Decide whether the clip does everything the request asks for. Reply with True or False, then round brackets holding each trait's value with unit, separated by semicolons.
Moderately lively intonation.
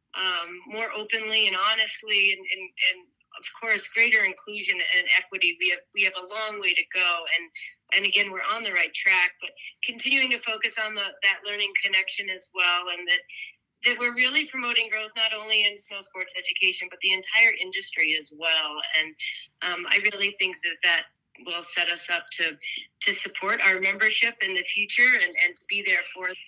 True (4.1 semitones)